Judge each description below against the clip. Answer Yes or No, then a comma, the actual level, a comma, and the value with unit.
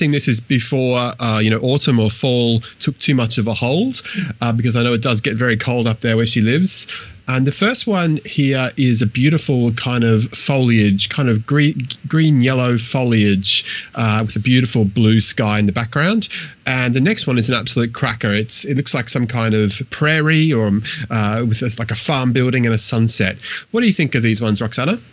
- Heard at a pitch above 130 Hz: No, low, 125 Hz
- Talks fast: Yes, fast, 215 wpm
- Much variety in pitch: No, average, 3.9 semitones